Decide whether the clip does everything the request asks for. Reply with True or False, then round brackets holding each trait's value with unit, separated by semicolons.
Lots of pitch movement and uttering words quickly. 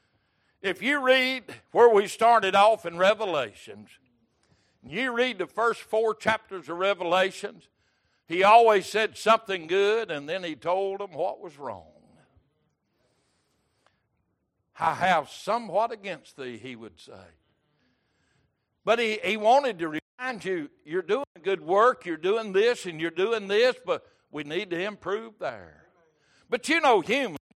False (5.9 semitones; 145 wpm)